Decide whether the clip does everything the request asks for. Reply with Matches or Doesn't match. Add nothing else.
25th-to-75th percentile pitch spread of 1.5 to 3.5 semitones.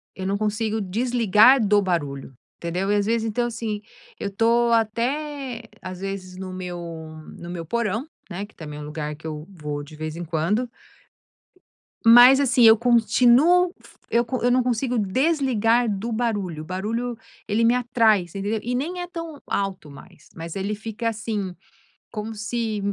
Doesn't match